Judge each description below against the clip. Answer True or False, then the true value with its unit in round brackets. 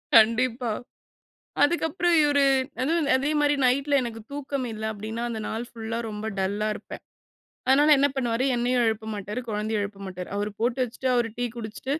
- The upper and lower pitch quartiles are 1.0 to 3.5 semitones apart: False (4.1 semitones)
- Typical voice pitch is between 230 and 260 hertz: True (240 Hz)